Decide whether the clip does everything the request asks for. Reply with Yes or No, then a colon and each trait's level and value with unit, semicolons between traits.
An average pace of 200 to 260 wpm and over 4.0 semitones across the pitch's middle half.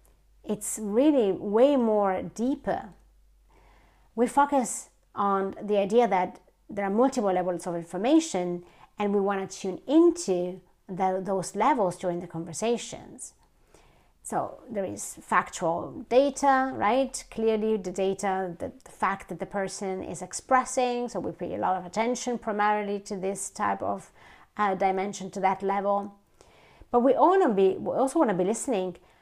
No: average, 150 wpm; average, 4.6 semitones